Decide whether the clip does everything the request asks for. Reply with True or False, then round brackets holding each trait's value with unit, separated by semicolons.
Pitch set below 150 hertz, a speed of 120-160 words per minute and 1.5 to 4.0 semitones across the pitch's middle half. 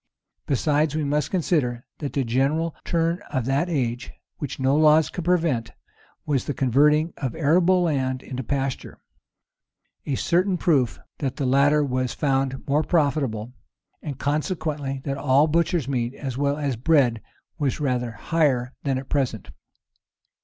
True (140 Hz; 145 wpm; 3.0 semitones)